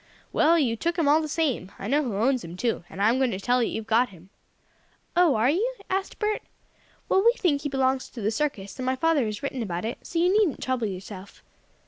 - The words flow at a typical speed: No, fast, 240 wpm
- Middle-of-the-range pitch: No, very high, 260 Hz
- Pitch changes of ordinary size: No, wide, 6.7 semitones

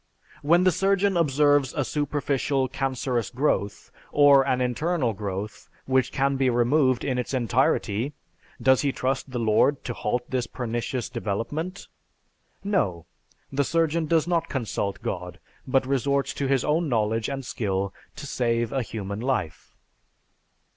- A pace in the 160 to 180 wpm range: No, average, 145 wpm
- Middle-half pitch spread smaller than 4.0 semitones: Yes, average, 3.6 semitones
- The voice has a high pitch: No, low, 130 Hz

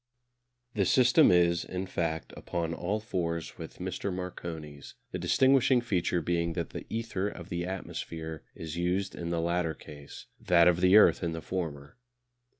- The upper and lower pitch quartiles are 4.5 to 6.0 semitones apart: No, narrow, 2.4 semitones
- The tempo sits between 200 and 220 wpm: No, average, 160 wpm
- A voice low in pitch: Yes, very low, 85 Hz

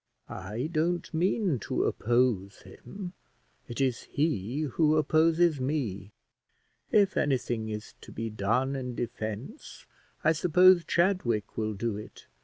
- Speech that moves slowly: Yes, slow, 125 wpm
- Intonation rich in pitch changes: Yes, wide, 6.7 semitones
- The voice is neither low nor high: No, low, 130 Hz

